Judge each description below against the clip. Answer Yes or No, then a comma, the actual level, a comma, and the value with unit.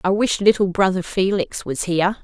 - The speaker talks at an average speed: Yes, average, 190 wpm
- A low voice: No, high, 190 Hz